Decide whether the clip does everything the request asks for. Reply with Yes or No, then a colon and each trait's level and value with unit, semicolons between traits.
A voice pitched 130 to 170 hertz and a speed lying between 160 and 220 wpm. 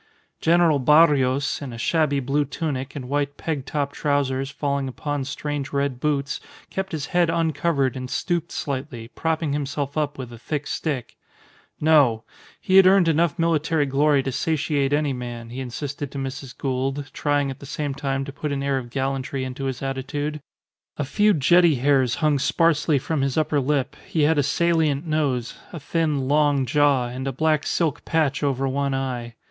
Yes: medium, 140 Hz; average, 180 wpm